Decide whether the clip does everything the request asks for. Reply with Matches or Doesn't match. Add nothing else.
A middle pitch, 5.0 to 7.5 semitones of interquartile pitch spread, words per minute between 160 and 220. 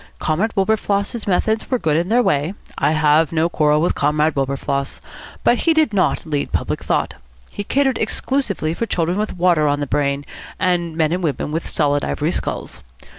Matches